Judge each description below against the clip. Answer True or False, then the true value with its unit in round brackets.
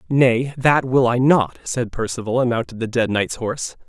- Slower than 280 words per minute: True (200 wpm)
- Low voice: True (120 Hz)